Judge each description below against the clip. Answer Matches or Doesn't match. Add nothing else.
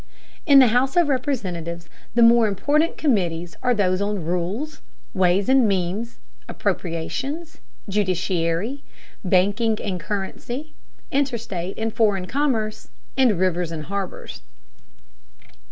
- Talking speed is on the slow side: Matches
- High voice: Matches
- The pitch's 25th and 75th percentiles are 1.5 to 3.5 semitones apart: Doesn't match